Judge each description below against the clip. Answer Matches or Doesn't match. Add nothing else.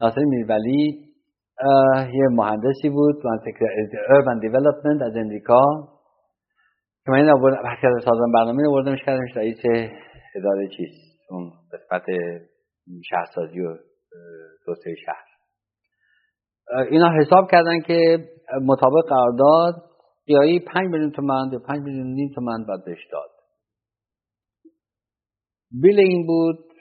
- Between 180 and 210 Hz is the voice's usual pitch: Doesn't match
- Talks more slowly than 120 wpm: Matches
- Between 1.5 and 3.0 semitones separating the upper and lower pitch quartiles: Doesn't match